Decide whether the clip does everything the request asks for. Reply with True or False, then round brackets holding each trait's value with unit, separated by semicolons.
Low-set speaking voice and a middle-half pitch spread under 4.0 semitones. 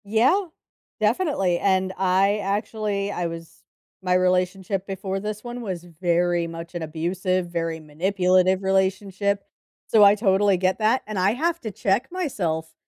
False (190 Hz; 2.6 semitones)